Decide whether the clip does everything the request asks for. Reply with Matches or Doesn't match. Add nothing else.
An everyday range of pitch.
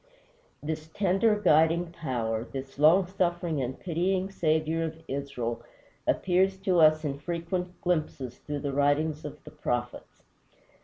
Matches